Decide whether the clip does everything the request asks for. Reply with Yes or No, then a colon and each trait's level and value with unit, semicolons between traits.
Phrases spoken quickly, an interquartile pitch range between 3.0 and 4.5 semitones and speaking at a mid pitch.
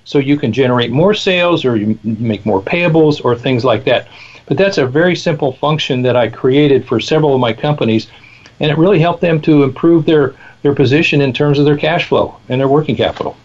Yes: fast, 220 wpm; average, 4.2 semitones; medium, 145 Hz